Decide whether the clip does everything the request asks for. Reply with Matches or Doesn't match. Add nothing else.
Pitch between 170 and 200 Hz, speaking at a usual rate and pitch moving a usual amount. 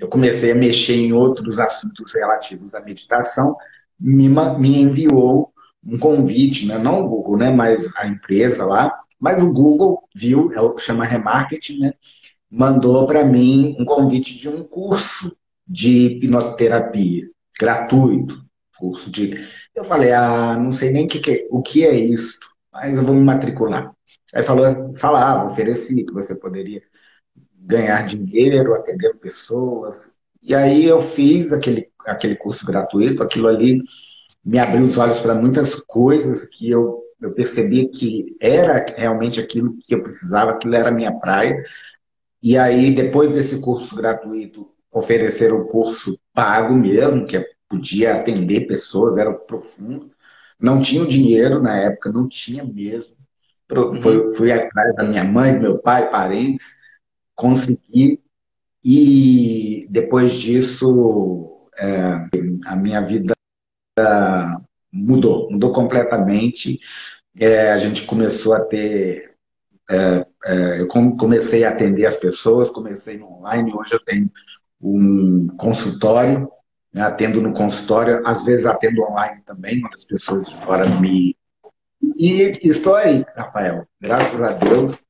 Doesn't match